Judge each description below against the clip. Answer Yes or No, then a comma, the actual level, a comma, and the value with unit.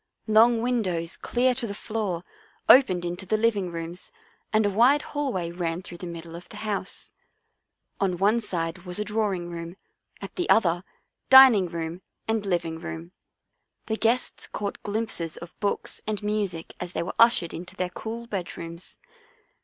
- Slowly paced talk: No, average, 160 wpm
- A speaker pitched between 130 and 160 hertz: No, high, 190 Hz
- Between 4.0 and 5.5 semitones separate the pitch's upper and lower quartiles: Yes, average, 4.4 semitones